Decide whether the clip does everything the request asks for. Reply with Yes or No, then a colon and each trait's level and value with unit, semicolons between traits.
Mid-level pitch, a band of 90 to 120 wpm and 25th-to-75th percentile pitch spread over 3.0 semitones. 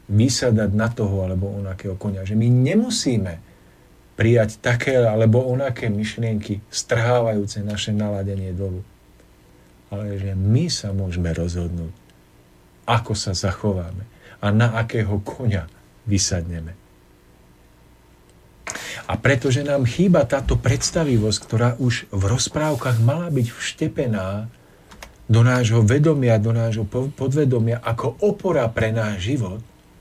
No: low, 110 Hz; slow, 110 wpm; average, 4.4 semitones